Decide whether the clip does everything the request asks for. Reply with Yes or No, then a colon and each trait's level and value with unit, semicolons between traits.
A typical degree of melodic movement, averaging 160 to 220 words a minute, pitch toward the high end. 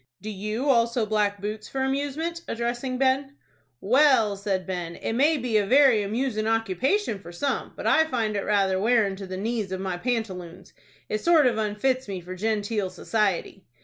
Yes: average, 4.7 semitones; average, 180 wpm; high, 220 Hz